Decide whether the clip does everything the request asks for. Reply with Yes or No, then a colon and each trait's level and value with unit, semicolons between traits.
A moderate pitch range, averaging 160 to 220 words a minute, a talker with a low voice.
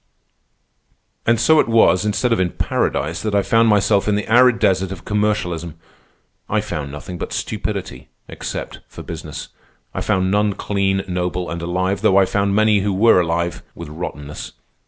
Yes: average, 3.5 semitones; average, 165 wpm; very low, 95 Hz